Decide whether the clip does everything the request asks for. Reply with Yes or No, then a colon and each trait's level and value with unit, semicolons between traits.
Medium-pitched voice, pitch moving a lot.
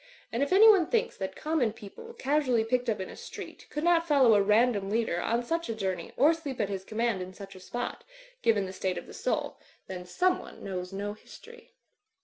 No: high, 230 Hz; wide, 7.7 semitones